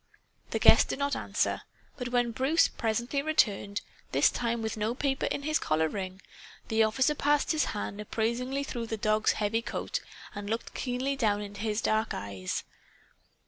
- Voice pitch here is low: No, high, 225 Hz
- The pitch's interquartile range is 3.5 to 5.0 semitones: Yes, average, 4.3 semitones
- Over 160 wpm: Yes, average, 170 wpm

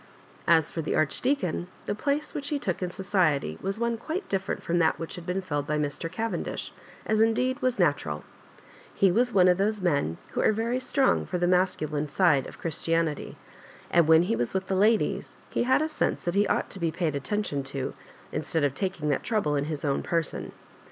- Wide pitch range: Yes, wide, 5.9 semitones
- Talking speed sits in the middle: No, fast, 210 wpm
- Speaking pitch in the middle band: Yes, medium, 180 Hz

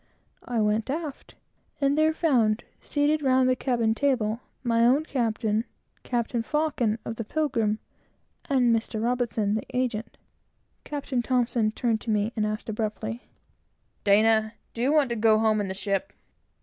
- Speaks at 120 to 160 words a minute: Yes, average, 150 wpm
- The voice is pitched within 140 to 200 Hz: No, high, 235 Hz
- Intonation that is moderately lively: Yes, average, 3.3 semitones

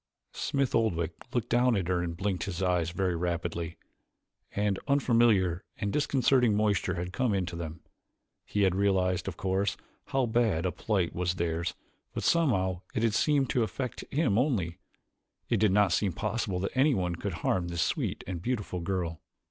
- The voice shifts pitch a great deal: No, average, 4.8 semitones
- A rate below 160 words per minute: No, average, 170 wpm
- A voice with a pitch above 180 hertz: No, very low, 95 Hz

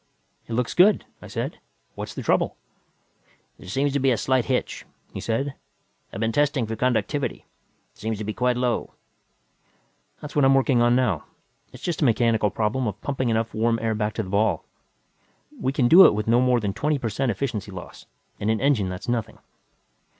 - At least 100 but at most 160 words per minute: No, average, 200 wpm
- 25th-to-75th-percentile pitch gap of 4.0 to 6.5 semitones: No, average, 3.6 semitones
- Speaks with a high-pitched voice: No, low, 120 Hz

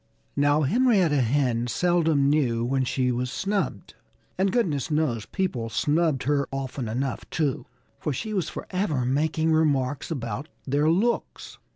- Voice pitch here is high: No, medium, 145 Hz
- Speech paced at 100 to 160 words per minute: Yes, average, 140 wpm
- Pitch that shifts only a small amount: No, average, 4.2 semitones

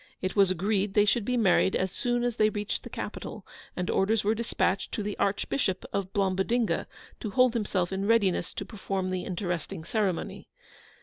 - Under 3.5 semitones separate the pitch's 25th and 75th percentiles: Yes, average, 2.8 semitones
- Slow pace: No, average, 180 wpm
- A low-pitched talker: No, high, 200 Hz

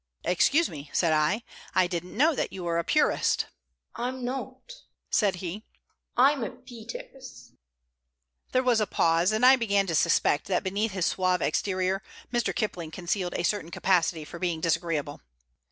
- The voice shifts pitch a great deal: Yes, wide, 5.8 semitones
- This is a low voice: No, medium, 185 Hz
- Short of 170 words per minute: Yes, average, 160 wpm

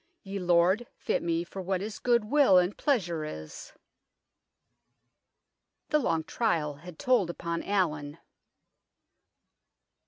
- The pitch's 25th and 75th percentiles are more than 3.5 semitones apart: Yes, average, 4.2 semitones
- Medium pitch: Yes, medium, 180 Hz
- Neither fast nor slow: No, slow, 115 wpm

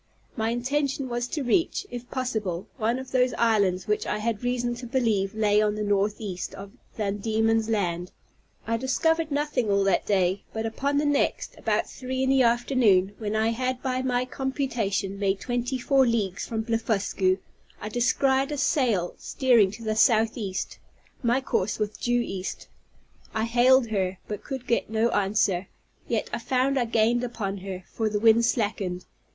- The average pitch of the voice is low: No, high, 225 Hz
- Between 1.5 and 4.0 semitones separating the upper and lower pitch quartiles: Yes, average, 3.7 semitones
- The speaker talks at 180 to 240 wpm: No, average, 170 wpm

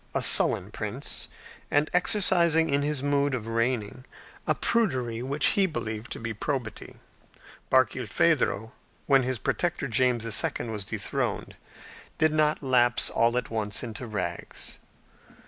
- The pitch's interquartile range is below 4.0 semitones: No, average, 4.8 semitones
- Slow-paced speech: Yes, slow, 130 wpm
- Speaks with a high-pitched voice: No, low, 130 Hz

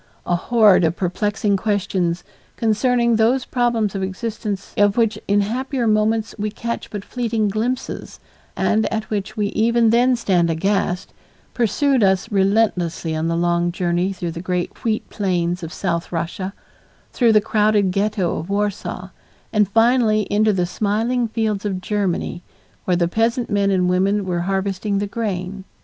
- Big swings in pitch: No, average, 3.4 semitones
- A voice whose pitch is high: Yes, high, 205 Hz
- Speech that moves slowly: No, average, 155 wpm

